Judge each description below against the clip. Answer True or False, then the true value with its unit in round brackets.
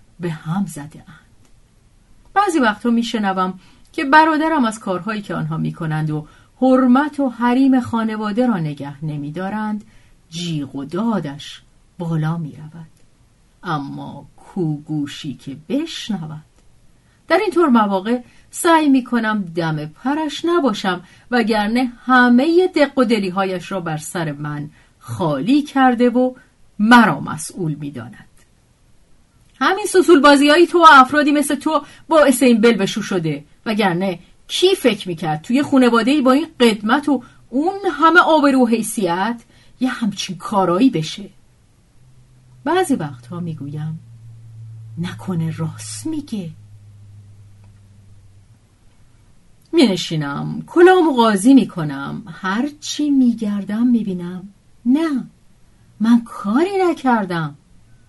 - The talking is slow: False (115 wpm)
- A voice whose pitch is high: True (210 Hz)